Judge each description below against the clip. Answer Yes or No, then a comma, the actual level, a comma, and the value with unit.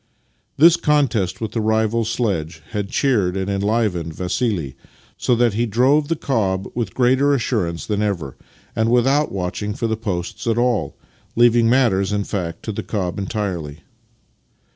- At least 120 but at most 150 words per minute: No, average, 160 wpm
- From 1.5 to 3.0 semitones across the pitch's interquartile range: No, average, 4.2 semitones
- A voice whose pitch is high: No, low, 110 Hz